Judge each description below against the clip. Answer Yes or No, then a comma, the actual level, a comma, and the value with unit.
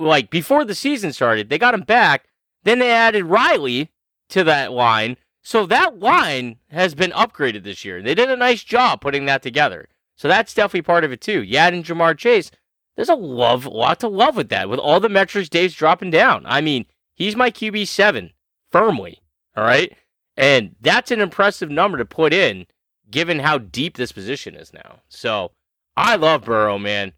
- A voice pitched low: No, medium, 170 Hz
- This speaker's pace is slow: No, average, 190 wpm